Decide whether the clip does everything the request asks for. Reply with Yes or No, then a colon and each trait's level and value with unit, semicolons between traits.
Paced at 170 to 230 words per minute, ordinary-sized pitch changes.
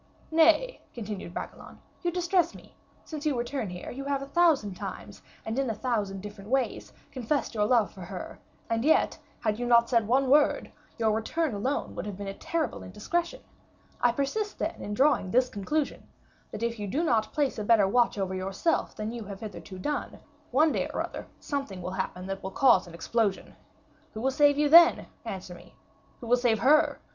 No: average, 195 wpm; wide, 6.0 semitones